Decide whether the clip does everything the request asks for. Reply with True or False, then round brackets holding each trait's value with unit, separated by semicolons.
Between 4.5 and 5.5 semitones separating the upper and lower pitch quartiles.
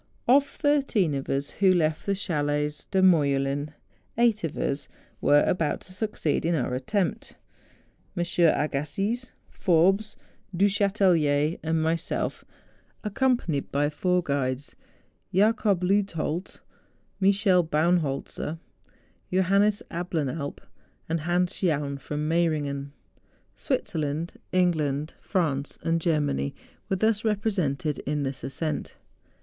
True (4.8 semitones)